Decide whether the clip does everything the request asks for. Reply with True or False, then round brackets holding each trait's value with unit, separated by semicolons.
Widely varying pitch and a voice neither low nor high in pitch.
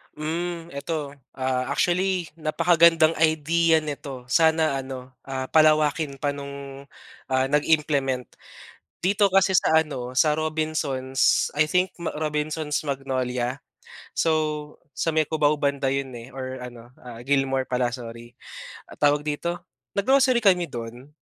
False (3.3 semitones; 150 Hz)